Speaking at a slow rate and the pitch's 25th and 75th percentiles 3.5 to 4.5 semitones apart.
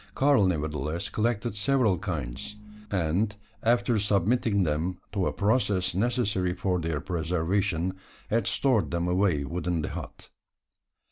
Yes: slow, 125 wpm; average, 4.0 semitones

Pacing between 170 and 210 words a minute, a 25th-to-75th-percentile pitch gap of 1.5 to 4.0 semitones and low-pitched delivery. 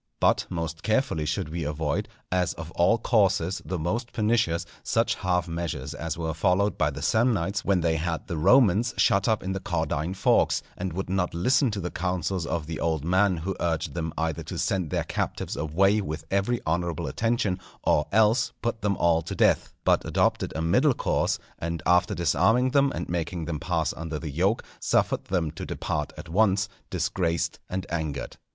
Yes: average, 185 wpm; average, 3.5 semitones; very low, 90 Hz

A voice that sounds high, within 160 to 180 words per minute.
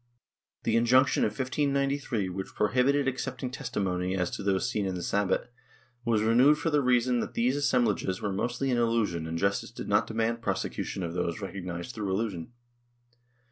No: low, 115 Hz; average, 170 wpm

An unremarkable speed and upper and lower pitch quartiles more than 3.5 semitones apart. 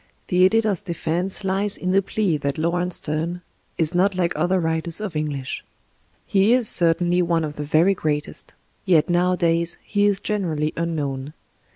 No: average, 160 wpm; average, 3.2 semitones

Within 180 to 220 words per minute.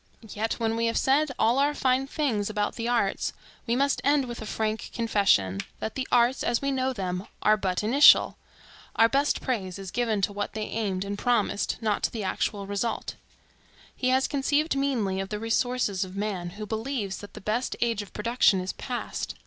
Yes: average, 195 wpm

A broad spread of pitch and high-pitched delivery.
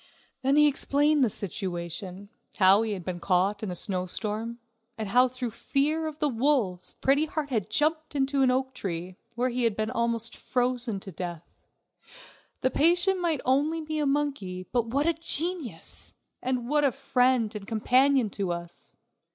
Yes: wide, 6.0 semitones; high, 245 Hz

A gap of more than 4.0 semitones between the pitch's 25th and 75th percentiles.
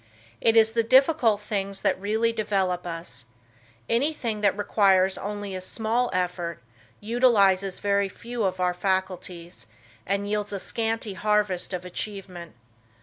No: average, 3.2 semitones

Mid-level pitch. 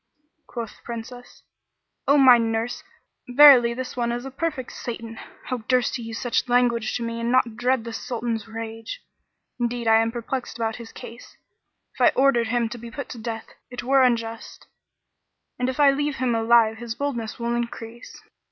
No: high, 235 Hz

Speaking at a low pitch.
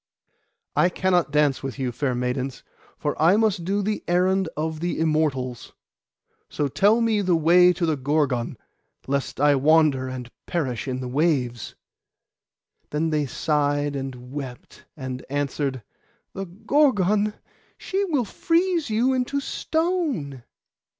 No: medium, 155 Hz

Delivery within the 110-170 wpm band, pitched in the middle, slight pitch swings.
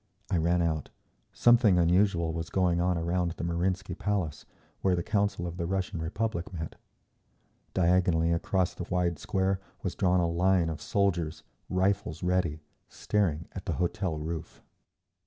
No: average, 150 wpm; very low, 90 Hz; narrow, 2.2 semitones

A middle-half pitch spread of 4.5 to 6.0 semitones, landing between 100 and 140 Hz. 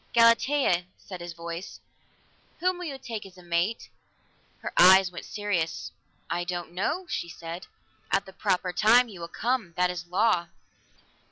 No: average, 4.8 semitones; medium, 185 Hz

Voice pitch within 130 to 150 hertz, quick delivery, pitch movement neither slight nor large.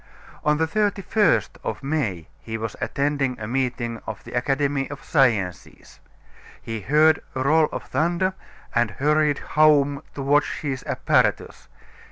No: medium, 140 Hz; average, 140 wpm; average, 4.2 semitones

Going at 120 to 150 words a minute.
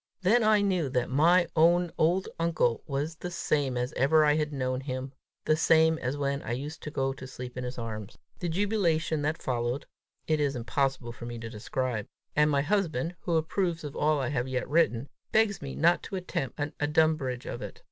No: fast, 205 wpm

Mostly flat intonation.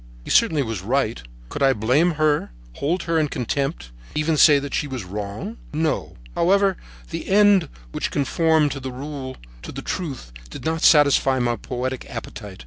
No: average, 4.0 semitones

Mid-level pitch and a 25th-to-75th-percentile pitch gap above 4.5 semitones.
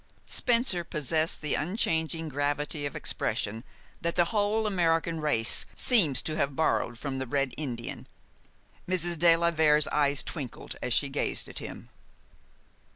No: medium, 155 Hz; average, 3.2 semitones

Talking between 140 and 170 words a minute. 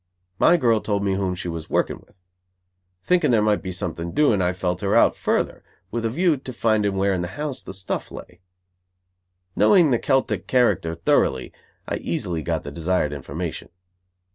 No: average, 180 wpm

